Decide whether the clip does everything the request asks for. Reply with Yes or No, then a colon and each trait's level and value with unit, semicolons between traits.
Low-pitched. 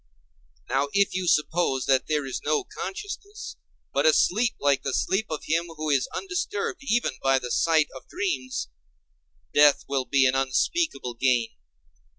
No: medium, 155 Hz